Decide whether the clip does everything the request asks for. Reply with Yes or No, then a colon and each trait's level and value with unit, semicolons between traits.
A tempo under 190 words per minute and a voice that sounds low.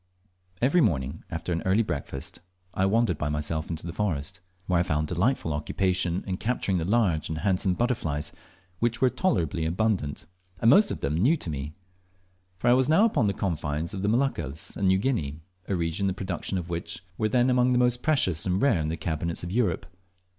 No: average, 200 wpm; very low, 95 Hz